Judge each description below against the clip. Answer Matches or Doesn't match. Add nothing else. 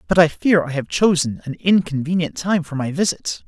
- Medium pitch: Matches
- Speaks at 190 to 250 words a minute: Matches